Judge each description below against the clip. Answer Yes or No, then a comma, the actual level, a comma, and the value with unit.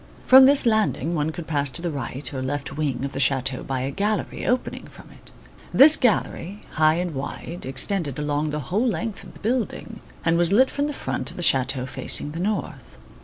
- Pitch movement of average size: No, wide, 7.1 semitones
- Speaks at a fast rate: Yes, fast, 210 wpm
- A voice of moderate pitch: Yes, medium, 160 Hz